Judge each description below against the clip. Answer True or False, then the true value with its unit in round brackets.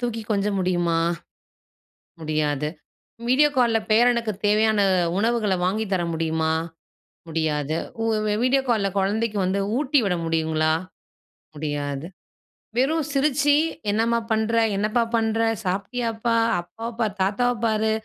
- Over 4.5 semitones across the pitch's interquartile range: True (5.5 semitones)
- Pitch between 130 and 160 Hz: False (215 Hz)